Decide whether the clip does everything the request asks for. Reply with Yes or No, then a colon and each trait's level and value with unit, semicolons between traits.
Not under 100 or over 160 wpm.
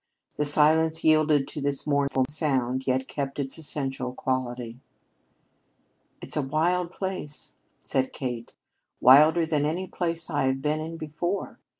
Yes: slow, 135 wpm